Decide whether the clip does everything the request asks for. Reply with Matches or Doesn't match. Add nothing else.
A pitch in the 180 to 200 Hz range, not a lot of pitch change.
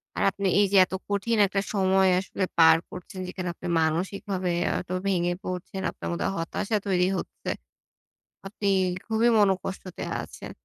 Matches